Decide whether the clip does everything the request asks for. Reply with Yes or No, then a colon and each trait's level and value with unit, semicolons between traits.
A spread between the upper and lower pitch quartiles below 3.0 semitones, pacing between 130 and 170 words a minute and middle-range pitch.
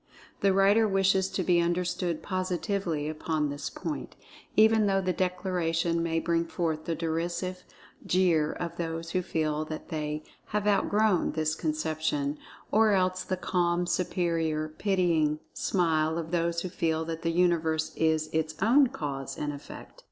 Yes: narrow, 2.6 semitones; average, 150 wpm; medium, 170 Hz